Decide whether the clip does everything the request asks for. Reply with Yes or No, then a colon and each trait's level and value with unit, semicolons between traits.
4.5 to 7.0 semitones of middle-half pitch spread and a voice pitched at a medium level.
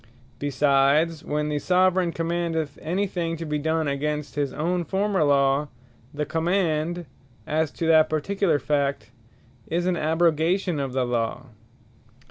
No: average, 3.0 semitones; medium, 155 Hz